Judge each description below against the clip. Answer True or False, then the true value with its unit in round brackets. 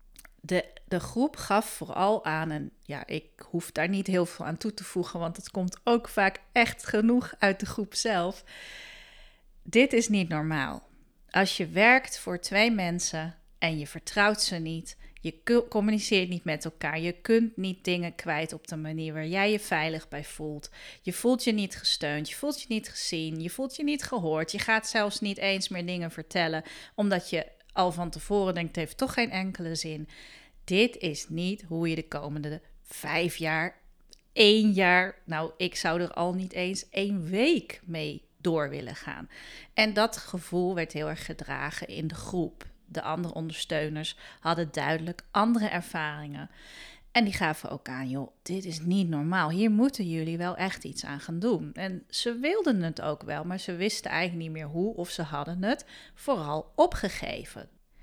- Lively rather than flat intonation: False (4.7 semitones)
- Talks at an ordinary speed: True (185 wpm)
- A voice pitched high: False (180 Hz)